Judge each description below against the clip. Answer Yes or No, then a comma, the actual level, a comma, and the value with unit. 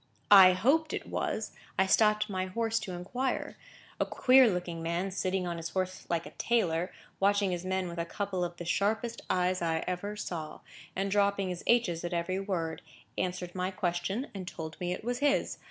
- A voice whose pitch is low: No, medium, 185 Hz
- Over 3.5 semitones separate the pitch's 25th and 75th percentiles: No, average, 2.8 semitones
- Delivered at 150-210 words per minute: Yes, average, 190 wpm